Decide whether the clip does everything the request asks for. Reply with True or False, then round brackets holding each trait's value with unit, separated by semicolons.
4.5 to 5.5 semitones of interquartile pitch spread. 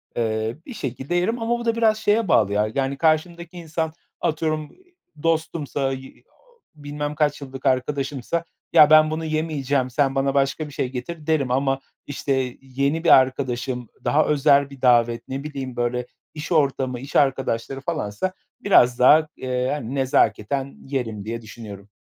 False (3.6 semitones)